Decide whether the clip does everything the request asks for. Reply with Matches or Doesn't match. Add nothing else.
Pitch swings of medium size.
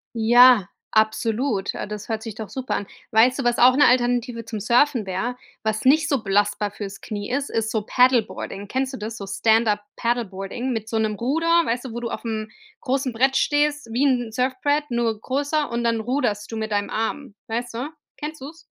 Matches